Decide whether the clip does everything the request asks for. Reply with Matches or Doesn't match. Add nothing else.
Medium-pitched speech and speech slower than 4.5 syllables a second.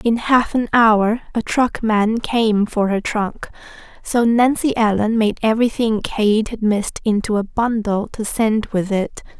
Doesn't match